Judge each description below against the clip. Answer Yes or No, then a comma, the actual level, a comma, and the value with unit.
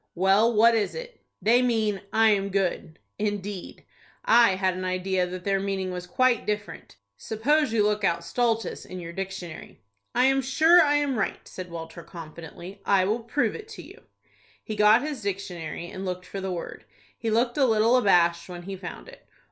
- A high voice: Yes, high, 200 Hz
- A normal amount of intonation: Yes, average, 4.1 semitones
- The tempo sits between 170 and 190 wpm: Yes, average, 185 wpm